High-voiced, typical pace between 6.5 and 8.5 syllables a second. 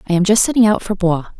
Yes: high, 200 Hz; 7.6 syllables/s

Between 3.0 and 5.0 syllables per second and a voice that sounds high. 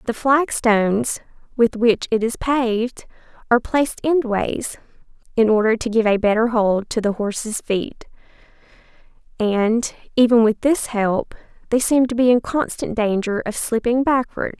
Yes: 4.5 syllables/s; high, 230 Hz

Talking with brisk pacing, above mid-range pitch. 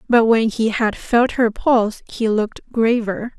No: average, 175 wpm; high, 225 Hz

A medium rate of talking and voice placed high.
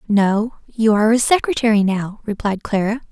Yes: average, 155 wpm; high, 215 Hz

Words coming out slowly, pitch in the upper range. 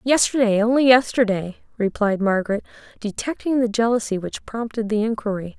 Yes: slow, 130 wpm; high, 220 Hz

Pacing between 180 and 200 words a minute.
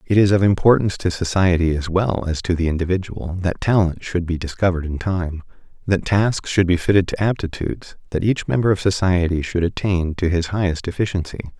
Yes: average, 190 wpm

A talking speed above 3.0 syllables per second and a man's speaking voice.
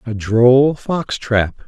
No: 2.7 syllables/s; male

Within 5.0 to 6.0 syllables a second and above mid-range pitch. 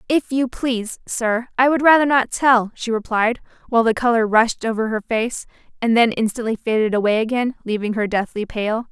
Yes: 5.2 syllables/s; high, 230 Hz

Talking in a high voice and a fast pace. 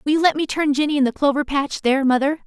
Yes: very high, 285 Hz; fast, 290 wpm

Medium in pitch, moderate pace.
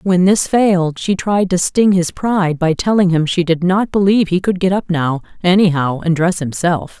No: medium, 180 Hz; fast, 215 wpm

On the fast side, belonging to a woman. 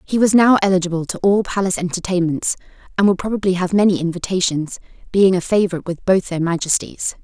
No: average, 175 wpm; female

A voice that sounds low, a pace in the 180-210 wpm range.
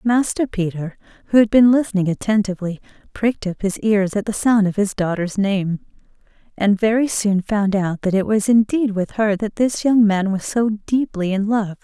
No: high, 205 Hz; average, 195 wpm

